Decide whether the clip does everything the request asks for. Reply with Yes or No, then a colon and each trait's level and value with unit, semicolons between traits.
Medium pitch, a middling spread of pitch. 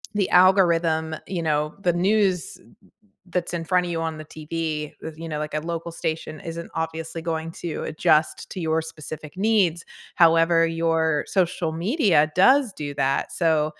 No: medium, 165 Hz; narrow, 1.8 semitones